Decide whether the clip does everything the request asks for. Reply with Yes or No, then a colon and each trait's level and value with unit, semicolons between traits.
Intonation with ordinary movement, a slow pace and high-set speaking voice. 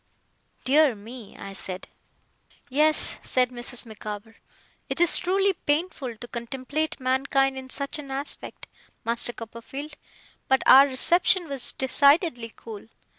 Yes: average, 4.0 semitones; slow, 125 wpm; very high, 265 Hz